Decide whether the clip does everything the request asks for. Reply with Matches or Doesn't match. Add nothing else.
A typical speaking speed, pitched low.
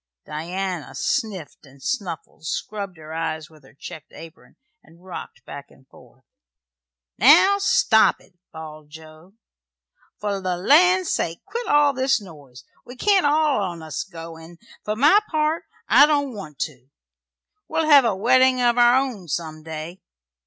Doesn't match